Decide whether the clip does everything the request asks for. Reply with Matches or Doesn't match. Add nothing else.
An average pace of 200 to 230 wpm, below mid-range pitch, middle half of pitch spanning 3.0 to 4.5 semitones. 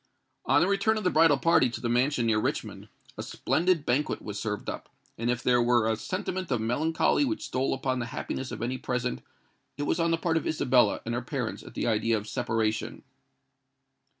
Doesn't match